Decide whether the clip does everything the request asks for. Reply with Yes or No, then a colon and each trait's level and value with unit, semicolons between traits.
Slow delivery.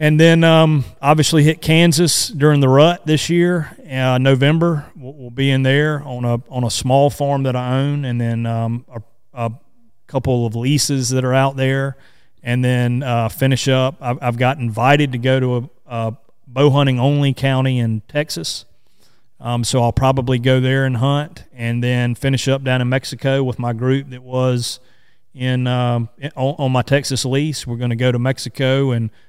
No: average, 190 wpm